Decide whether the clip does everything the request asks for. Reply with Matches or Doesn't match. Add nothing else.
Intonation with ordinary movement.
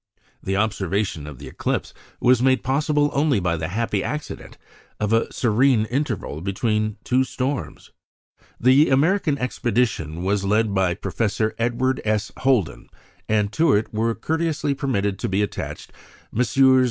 Matches